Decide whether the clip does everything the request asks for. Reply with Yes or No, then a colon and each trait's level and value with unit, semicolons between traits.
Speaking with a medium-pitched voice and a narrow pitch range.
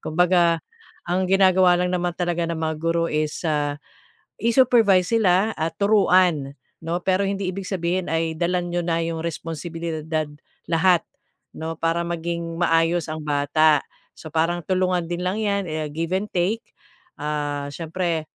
Yes: medium, 170 Hz; narrow, 2.3 semitones